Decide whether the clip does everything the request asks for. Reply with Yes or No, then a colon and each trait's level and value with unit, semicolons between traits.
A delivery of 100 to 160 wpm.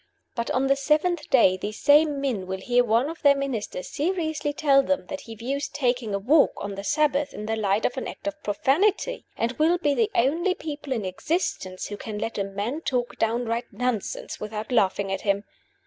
No: fast, 205 wpm